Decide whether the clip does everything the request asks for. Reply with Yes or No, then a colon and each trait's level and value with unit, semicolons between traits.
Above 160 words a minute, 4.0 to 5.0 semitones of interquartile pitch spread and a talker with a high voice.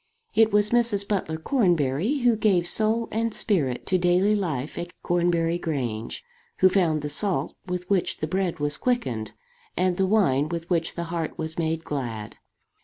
No: average, 170 wpm; average, 4.7 semitones; medium, 175 Hz